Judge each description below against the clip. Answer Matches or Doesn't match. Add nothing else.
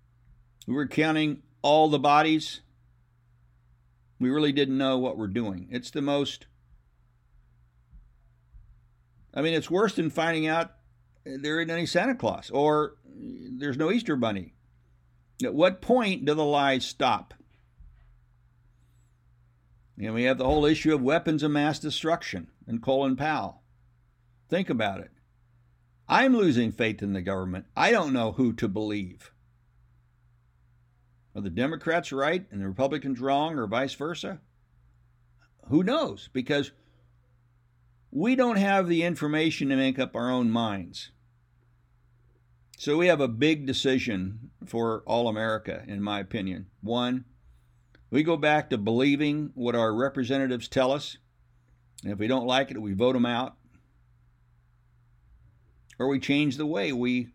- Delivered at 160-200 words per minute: Doesn't match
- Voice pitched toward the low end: Matches